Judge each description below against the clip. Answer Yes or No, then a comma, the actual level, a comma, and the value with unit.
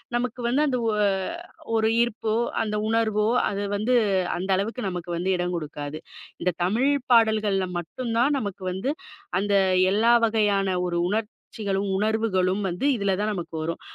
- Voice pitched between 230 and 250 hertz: No, high, 205 Hz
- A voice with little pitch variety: No, average, 3.3 semitones